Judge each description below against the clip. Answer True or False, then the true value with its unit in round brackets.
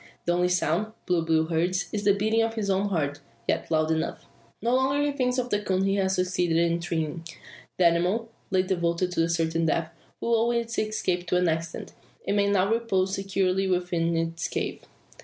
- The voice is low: False (185 Hz)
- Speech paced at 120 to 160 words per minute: False (195 wpm)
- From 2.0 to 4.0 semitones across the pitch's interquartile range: True (3.6 semitones)